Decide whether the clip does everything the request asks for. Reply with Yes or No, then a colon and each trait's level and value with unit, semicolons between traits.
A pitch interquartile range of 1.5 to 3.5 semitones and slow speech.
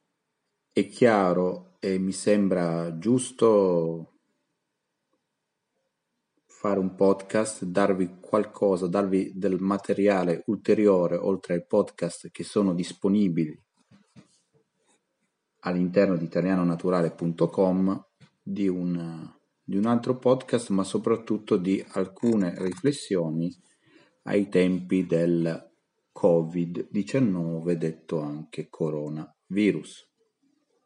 Yes: average, 2.7 semitones; slow, 80 wpm